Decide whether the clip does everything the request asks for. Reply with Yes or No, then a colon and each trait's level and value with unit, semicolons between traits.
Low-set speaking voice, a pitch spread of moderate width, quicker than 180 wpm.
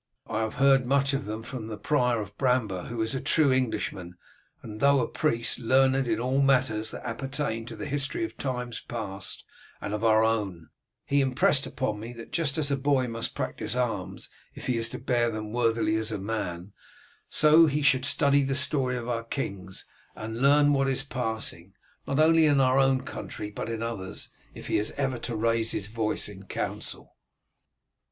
Yes: low, 120 Hz; average, 3.7 semitones; average, 195 wpm